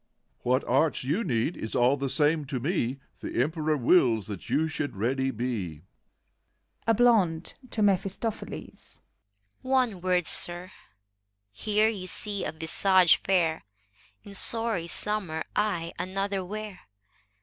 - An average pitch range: No, wide, 7.0 semitones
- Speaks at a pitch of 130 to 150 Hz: No, medium, 165 Hz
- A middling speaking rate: No, slow, 130 wpm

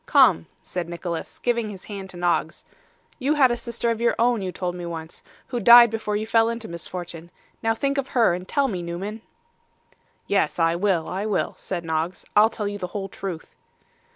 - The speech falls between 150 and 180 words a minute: No, average, 200 wpm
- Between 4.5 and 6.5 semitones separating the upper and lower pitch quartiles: Yes, average, 4.9 semitones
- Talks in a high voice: Yes, high, 200 Hz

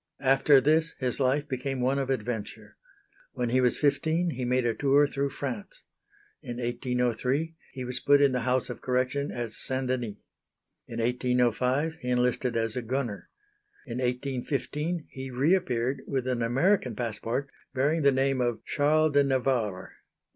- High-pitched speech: No, low, 130 Hz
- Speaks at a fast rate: No, average, 160 wpm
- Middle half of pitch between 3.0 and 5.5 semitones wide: No, narrow, 2.4 semitones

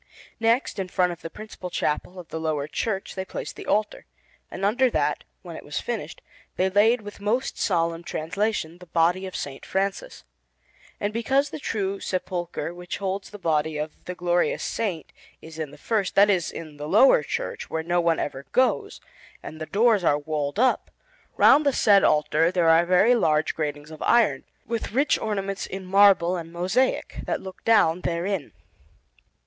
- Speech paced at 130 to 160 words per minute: No, average, 180 wpm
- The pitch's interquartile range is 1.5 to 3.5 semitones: No, average, 4.2 semitones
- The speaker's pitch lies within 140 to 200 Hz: Yes, medium, 185 Hz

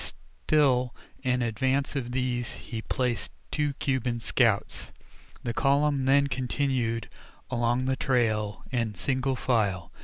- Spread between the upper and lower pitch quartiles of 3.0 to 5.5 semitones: No, narrow, 2.4 semitones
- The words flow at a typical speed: No, slow, 120 wpm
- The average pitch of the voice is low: Yes, low, 125 Hz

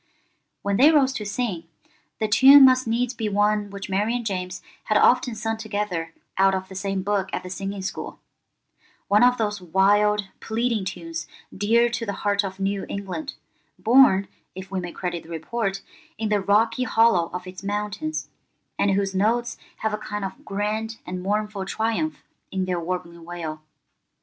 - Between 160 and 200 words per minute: Yes, average, 170 wpm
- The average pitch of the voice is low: No, high, 205 Hz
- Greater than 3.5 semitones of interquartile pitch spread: No, average, 2.8 semitones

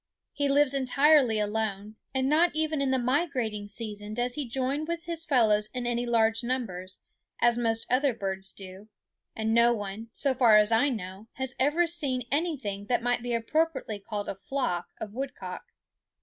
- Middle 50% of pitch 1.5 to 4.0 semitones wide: No, average, 4.5 semitones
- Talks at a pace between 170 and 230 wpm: Yes, average, 175 wpm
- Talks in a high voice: Yes, high, 240 Hz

